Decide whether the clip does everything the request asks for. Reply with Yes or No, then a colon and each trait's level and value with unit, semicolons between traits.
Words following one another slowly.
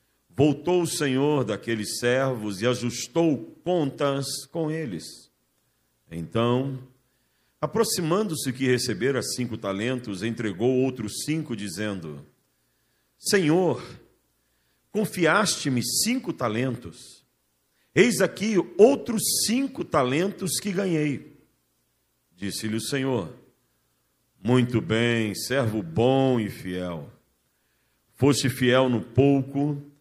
Yes: slow, 90 wpm